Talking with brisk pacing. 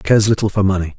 Yes: fast, 245 wpm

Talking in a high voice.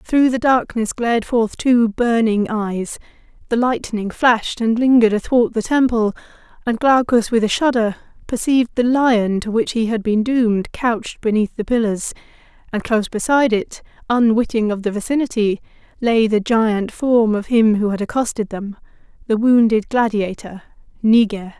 Yes: high, 225 Hz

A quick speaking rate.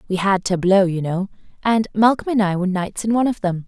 Yes: fast, 245 wpm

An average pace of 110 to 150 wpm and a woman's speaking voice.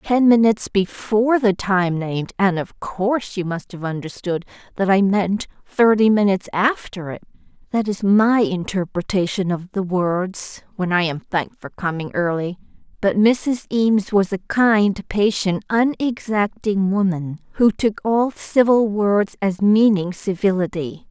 Yes: average, 145 wpm; female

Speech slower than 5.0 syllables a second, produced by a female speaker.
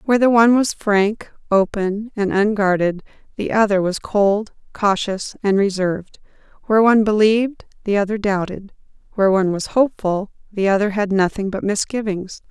No: 5.3 syllables/s; female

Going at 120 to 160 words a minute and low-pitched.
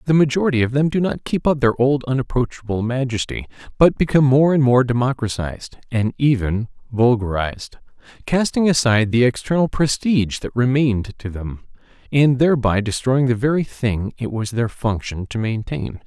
Yes: average, 155 wpm; low, 125 Hz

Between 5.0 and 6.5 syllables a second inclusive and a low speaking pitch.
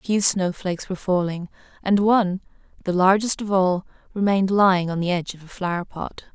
No: 6.1 syllables/s; medium, 185 Hz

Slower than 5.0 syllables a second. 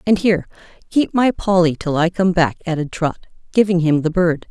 No: 5.5 syllables/s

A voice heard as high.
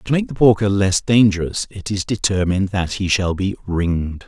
No: low, 100 Hz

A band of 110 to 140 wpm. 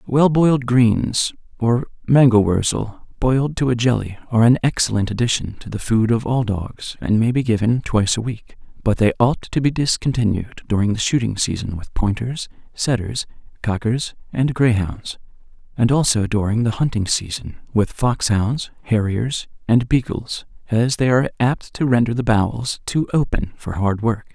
No: average, 160 wpm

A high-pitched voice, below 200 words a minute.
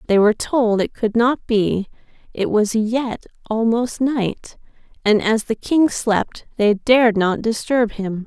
Yes: high, 225 Hz; average, 160 wpm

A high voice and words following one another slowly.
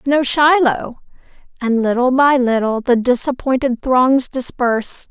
Yes: very high, 255 Hz; slow, 120 wpm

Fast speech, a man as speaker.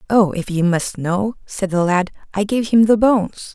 No: fast, 220 wpm; female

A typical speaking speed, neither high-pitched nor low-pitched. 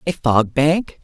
Yes: average, 175 wpm; medium, 150 Hz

